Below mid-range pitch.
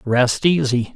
Yes: low, 130 Hz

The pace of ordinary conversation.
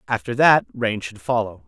Yes: average, 180 wpm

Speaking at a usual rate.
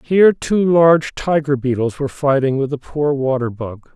Yes: average, 180 wpm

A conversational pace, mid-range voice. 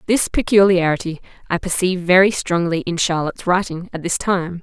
Yes: average, 155 wpm; medium, 180 Hz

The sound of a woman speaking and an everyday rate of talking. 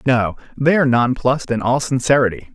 No: male; average, 165 wpm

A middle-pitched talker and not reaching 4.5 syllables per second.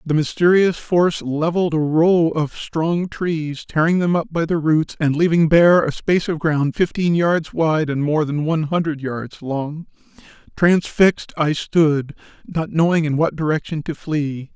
Yes: medium, 160 Hz; 4.3 syllables/s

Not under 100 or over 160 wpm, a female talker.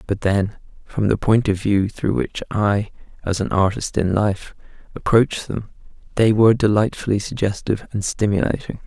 No: average, 155 wpm; male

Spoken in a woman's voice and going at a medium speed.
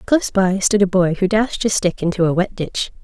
No: female; fast, 255 wpm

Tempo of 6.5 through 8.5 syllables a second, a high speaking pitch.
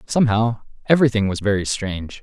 No: 6.6 syllables/s; low, 110 Hz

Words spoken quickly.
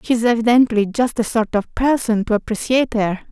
No: average, 180 wpm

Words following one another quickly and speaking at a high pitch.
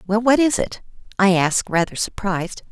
No: average, 175 wpm; high, 200 Hz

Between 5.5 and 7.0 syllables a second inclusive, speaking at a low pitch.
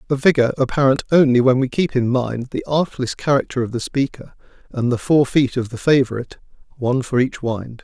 Yes: 5.7 syllables/s; low, 130 Hz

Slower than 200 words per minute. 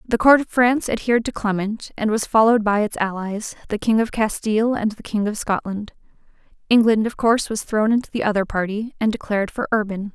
No: fast, 205 wpm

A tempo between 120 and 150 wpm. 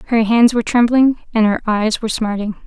No: fast, 205 wpm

